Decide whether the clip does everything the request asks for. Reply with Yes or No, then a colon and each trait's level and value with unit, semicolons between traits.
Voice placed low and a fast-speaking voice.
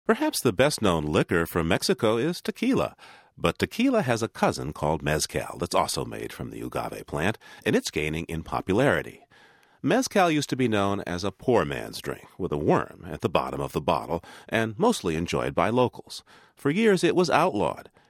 No: low, 115 Hz; average, 190 wpm